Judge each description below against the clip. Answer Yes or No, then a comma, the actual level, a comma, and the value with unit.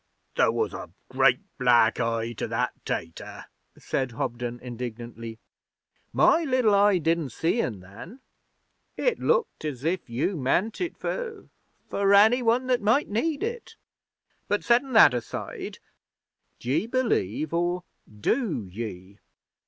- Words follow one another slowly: Yes, slow, 130 wpm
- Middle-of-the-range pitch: Yes, medium, 165 Hz